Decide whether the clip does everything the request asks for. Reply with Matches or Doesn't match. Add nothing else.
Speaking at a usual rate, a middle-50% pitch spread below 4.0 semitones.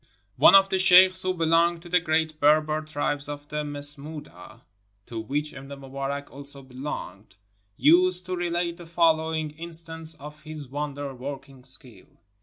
Matches